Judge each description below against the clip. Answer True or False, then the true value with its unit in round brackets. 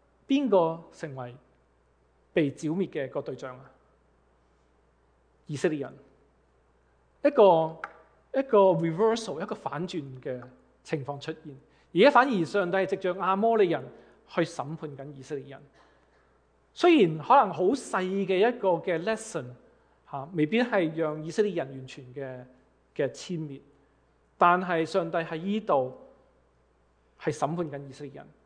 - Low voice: False (155 Hz)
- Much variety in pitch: True (6.8 semitones)